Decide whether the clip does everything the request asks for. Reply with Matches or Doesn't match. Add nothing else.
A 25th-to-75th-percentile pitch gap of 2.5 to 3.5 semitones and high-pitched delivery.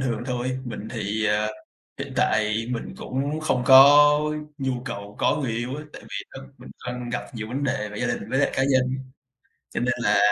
Doesn't match